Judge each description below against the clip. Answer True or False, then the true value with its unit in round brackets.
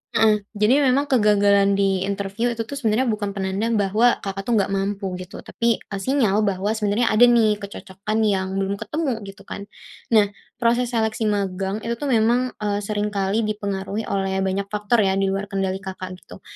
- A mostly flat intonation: True (2.2 semitones)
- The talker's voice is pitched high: True (205 Hz)